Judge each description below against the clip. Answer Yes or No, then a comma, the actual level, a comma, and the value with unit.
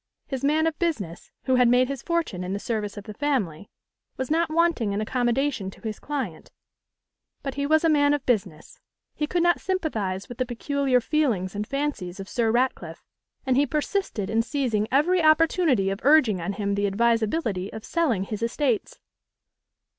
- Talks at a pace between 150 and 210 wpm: Yes, average, 180 wpm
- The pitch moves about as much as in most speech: No, wide, 6.3 semitones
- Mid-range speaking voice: No, very high, 250 Hz